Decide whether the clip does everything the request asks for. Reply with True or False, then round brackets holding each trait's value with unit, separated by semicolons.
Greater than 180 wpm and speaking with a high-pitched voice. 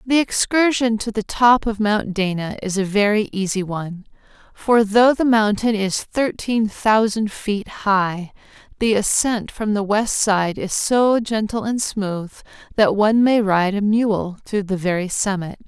False (165 wpm; 210 Hz)